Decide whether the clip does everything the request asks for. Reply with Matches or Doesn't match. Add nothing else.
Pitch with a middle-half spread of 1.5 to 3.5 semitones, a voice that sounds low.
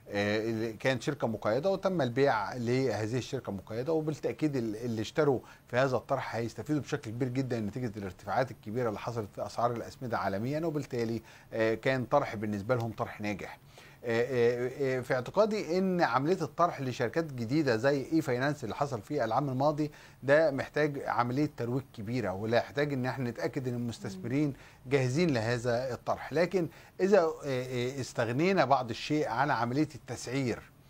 Doesn't match